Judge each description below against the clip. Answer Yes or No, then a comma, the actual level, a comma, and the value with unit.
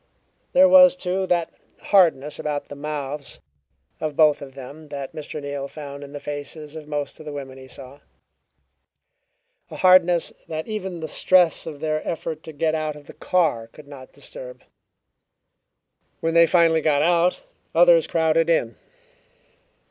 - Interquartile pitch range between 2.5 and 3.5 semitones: Yes, average, 2.9 semitones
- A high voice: No, medium, 155 Hz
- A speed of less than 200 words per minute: Yes, average, 155 wpm